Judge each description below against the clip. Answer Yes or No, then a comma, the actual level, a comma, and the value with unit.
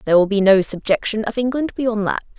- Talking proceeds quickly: Yes, fast, 225 wpm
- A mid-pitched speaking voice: No, high, 215 Hz